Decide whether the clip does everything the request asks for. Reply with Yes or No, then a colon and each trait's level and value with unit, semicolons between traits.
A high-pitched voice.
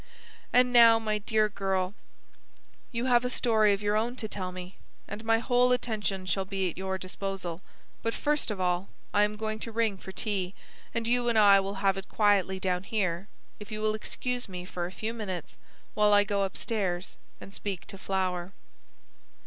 Yes: high, 205 Hz